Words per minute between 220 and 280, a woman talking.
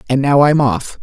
Yes: fast, 235 wpm; female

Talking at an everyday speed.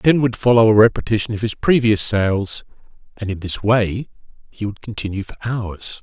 Yes: average, 180 wpm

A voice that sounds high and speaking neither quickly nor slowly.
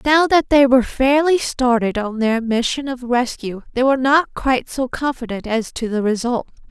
Yes: very high, 250 Hz; average, 190 wpm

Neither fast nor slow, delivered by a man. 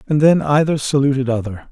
Yes: average, 175 wpm; male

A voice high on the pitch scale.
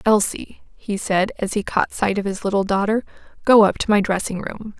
Yes: high, 205 Hz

